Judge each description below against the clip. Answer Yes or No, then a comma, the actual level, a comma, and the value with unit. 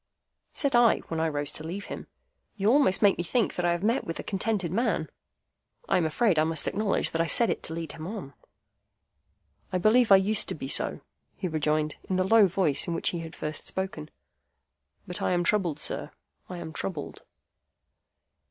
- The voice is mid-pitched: Yes, medium, 180 Hz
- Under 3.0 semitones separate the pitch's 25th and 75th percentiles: No, average, 4.3 semitones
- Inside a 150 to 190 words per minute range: No, average, 200 wpm